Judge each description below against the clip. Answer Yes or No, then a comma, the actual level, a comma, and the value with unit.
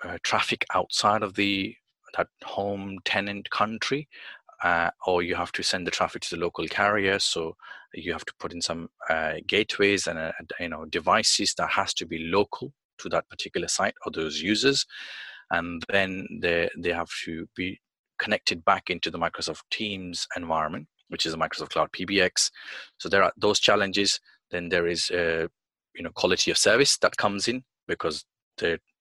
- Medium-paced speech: Yes, average, 180 wpm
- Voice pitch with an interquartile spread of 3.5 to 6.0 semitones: No, average, 2.9 semitones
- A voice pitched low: Yes, low, 100 Hz